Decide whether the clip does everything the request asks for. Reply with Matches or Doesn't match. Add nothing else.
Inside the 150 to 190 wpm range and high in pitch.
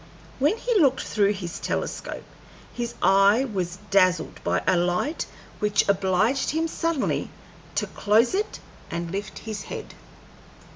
Doesn't match